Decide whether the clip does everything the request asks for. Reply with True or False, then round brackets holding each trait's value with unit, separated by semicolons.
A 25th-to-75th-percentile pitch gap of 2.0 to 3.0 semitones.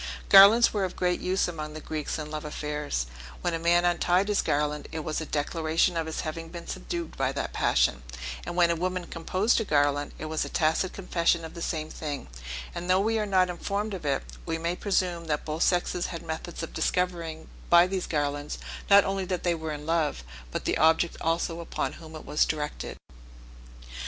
True (2.7 semitones)